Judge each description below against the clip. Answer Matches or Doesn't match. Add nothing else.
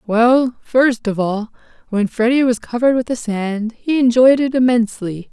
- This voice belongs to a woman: Matches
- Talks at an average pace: Matches